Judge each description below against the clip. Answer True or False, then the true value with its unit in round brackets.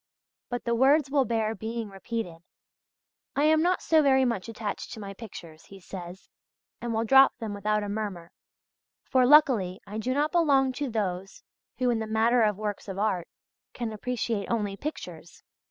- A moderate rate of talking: True (175 wpm)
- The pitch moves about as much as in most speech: True (4.1 semitones)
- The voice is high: True (225 Hz)